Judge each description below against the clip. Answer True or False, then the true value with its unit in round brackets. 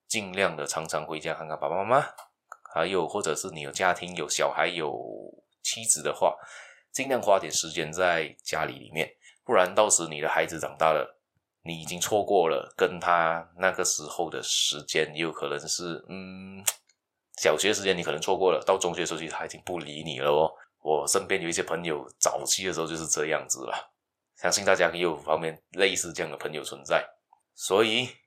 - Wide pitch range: False (3.1 semitones)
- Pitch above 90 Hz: False (85 Hz)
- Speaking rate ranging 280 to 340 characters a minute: True (285 characters per minute)